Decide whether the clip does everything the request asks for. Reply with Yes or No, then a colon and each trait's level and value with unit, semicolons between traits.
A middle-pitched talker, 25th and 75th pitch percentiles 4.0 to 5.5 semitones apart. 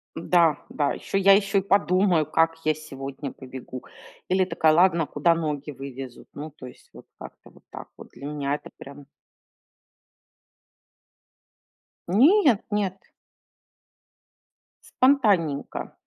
Yes: medium, 160 Hz; average, 5.2 semitones